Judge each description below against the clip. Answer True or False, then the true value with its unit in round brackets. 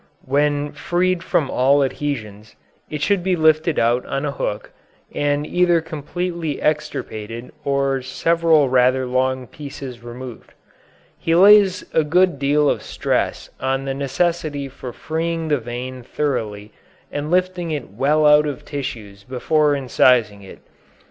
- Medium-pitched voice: True (145 Hz)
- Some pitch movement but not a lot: True (3.7 semitones)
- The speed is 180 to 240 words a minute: False (135 wpm)